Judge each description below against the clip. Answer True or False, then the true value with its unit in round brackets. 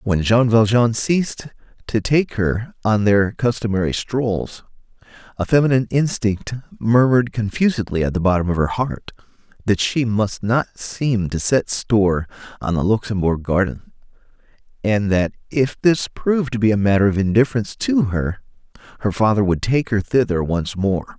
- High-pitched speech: False (110 Hz)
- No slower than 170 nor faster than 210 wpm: False (155 wpm)